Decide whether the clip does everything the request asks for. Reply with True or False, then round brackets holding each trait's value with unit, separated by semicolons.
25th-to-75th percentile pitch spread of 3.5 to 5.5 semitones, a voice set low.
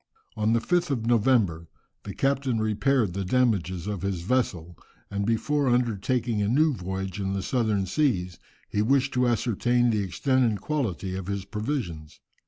True (4.8 semitones; 110 Hz)